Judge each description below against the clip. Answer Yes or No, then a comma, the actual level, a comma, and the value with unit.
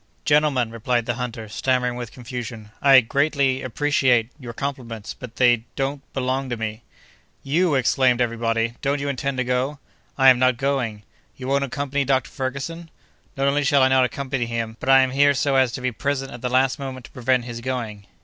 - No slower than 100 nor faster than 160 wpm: No, average, 180 wpm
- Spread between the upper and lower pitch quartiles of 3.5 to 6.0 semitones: No, narrow, 2.4 semitones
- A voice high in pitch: No, low, 130 Hz